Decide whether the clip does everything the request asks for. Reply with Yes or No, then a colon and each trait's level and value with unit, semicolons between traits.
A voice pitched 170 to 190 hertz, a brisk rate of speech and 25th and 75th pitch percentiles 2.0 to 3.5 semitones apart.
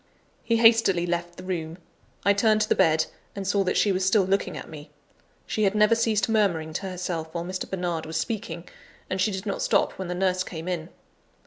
Yes: medium, 185 Hz; fast, 215 wpm; average, 3.1 semitones